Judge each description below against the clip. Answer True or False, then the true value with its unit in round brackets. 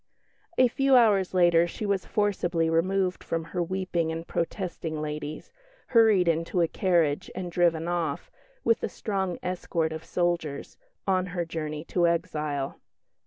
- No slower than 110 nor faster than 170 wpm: True (145 wpm)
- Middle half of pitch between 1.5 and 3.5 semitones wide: True (2.6 semitones)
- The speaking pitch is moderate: True (175 Hz)